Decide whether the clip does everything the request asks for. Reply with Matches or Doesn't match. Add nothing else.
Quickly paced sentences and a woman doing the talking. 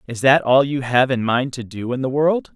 Doesn't match